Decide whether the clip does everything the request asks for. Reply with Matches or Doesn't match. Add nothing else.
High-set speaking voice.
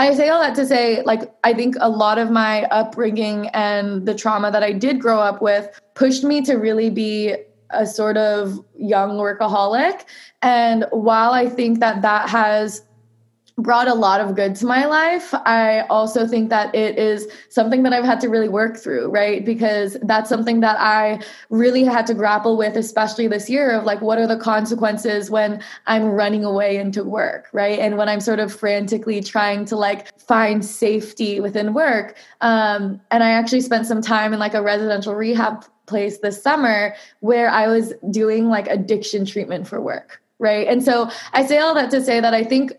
Matches